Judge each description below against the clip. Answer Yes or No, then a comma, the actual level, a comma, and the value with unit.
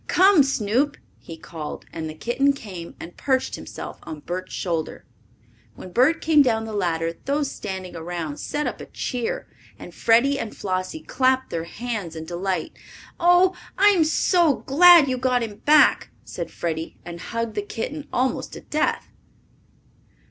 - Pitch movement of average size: No, wide, 8.4 semitones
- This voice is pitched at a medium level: No, high, 230 Hz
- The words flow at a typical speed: Yes, average, 155 wpm